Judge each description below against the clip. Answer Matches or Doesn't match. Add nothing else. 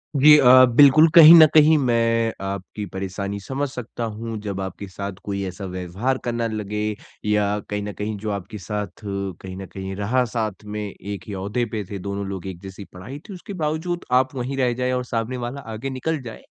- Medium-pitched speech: Doesn't match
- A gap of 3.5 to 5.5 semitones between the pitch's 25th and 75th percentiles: Matches